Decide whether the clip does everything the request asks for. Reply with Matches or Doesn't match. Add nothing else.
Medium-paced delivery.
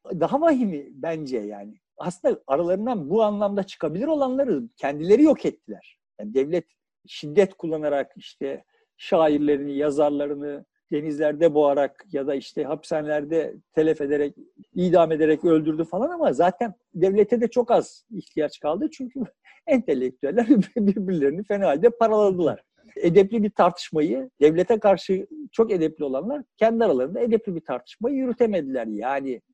Matches